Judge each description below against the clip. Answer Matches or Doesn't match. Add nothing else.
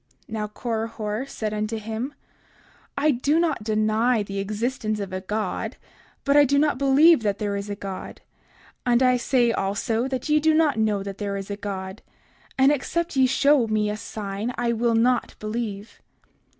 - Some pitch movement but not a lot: Matches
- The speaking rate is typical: Matches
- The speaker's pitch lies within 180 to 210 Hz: Doesn't match